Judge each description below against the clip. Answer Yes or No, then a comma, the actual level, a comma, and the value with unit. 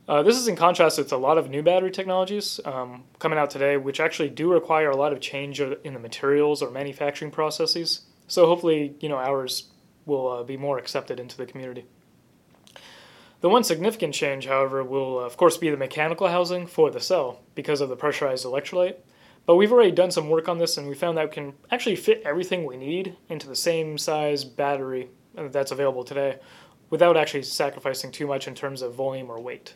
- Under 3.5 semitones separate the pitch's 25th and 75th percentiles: No, average, 3.9 semitones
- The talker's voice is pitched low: No, medium, 150 Hz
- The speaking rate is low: No, fast, 205 wpm